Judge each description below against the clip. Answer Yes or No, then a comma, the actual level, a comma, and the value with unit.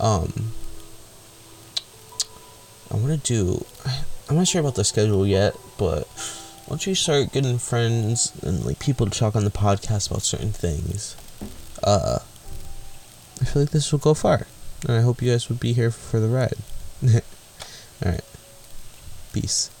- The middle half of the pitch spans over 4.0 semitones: No, average, 3.5 semitones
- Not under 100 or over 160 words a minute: Yes, average, 155 wpm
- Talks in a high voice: No, low, 110 Hz